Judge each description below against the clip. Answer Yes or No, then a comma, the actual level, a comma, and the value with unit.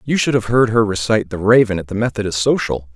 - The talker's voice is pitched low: Yes, low, 105 Hz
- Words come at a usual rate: No, fast, 245 wpm